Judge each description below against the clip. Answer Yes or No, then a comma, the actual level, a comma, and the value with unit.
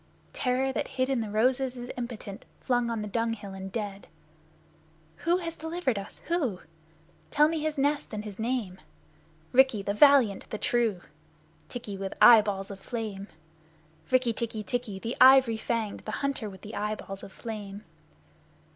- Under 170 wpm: Yes, average, 155 wpm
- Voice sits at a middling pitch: No, high, 230 Hz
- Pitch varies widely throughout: No, average, 4.1 semitones